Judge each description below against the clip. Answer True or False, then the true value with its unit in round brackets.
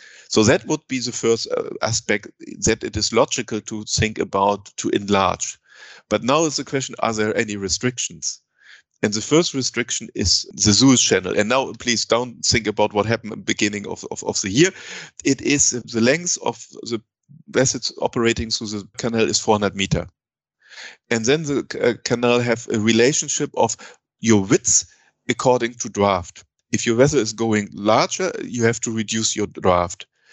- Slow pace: False (180 wpm)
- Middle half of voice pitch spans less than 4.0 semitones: True (2.9 semitones)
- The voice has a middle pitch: False (115 Hz)